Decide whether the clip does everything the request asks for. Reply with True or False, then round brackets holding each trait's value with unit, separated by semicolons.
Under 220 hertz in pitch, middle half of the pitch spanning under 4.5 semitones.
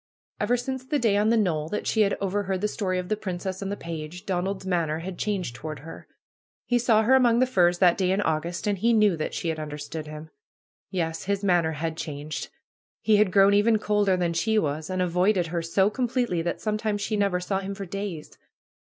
True (190 Hz; 4.0 semitones)